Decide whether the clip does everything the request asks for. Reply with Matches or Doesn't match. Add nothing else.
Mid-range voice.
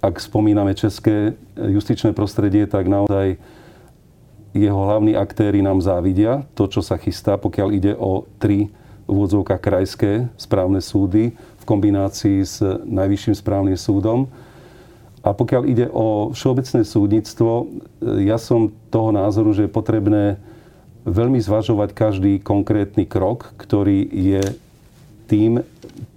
Doesn't match